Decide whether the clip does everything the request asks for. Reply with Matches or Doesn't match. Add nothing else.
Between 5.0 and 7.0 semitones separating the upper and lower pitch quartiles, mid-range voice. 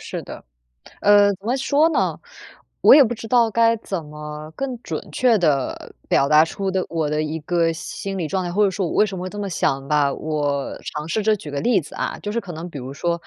Matches